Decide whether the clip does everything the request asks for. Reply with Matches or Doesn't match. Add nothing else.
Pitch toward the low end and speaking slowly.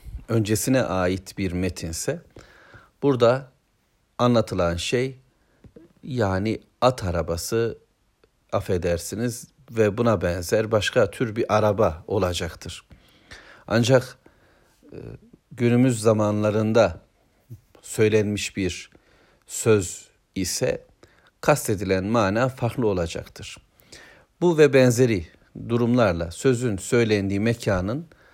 Matches